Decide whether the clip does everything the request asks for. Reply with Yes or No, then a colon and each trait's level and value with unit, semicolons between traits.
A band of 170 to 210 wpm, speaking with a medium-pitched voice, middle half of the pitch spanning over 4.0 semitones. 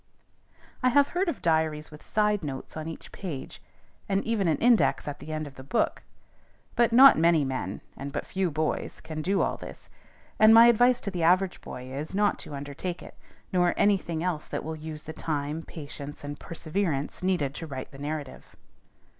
Yes: average, 195 wpm; medium, 160 Hz; average, 5.1 semitones